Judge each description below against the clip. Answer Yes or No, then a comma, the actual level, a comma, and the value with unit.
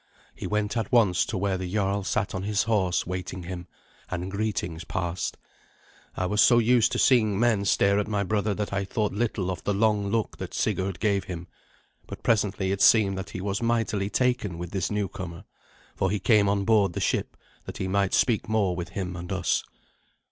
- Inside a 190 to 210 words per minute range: Yes, average, 200 wpm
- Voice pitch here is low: Yes, low, 100 Hz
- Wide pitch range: No, narrow, 2.4 semitones